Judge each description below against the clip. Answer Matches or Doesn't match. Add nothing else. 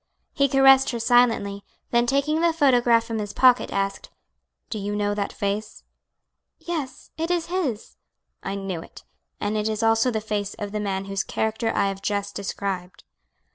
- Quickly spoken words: Doesn't match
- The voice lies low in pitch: Doesn't match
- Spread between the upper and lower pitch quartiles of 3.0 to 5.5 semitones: Matches